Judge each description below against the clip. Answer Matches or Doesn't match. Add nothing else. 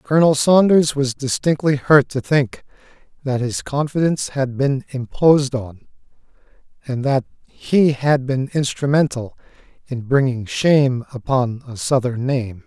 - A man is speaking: Matches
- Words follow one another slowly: Matches